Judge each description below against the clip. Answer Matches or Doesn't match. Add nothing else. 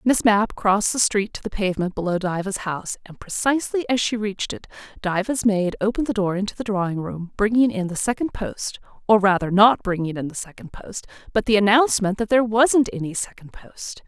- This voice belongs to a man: Doesn't match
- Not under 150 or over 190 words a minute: Doesn't match